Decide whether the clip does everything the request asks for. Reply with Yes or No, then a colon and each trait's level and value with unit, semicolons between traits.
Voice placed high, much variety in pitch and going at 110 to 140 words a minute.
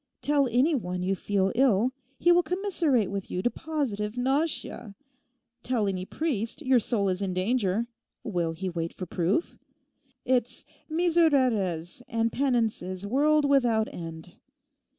Yes: high, 230 Hz; wide, 6.6 semitones; slow, 135 wpm